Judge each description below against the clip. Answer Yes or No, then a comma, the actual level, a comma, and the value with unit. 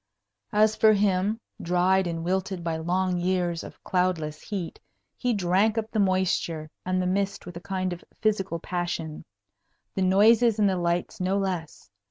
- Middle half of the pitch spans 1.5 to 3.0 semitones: Yes, narrow, 2.4 semitones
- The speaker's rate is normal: Yes, average, 165 wpm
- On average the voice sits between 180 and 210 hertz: Yes, medium, 185 Hz